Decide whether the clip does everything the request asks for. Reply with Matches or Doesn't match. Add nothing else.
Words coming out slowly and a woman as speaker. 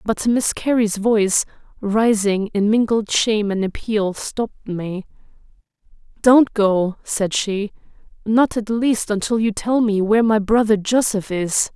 Doesn't match